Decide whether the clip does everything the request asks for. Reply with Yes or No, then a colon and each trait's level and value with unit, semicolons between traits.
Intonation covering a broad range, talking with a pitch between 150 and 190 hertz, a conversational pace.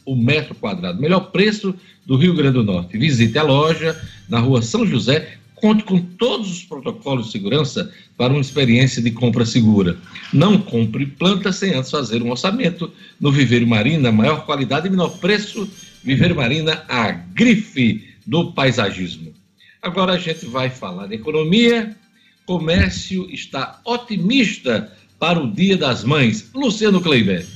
Yes: wide, 7.7 semitones; medium, 160 Hz; average, 150 wpm